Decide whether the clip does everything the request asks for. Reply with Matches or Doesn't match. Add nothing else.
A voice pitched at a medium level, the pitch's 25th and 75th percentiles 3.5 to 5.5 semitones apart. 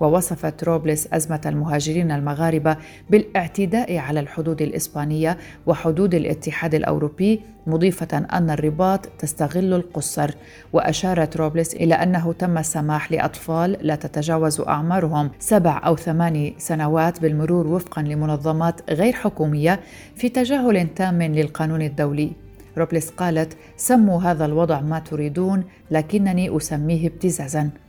Doesn't match